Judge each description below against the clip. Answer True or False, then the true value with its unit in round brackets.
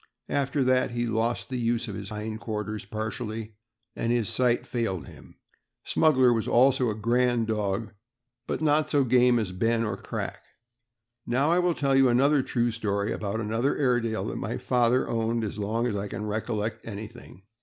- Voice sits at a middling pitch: False (115 Hz)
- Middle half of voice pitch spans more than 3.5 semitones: False (2.7 semitones)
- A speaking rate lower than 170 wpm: False (180 wpm)